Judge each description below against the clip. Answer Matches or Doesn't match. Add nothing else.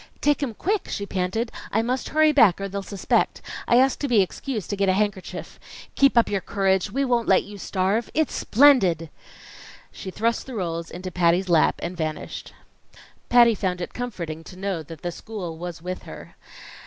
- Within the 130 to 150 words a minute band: Doesn't match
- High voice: Matches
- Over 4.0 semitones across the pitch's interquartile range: Matches